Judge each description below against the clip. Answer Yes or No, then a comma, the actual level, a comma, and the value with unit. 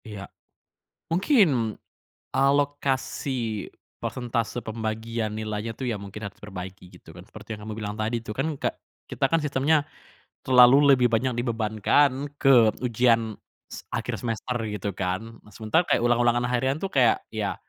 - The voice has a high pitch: No, low, 115 Hz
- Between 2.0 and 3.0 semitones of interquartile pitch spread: No, average, 3.5 semitones